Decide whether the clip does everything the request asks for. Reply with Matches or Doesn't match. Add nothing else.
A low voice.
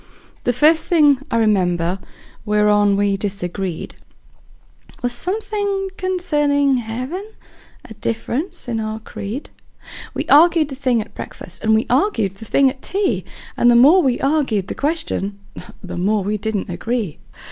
Doesn't match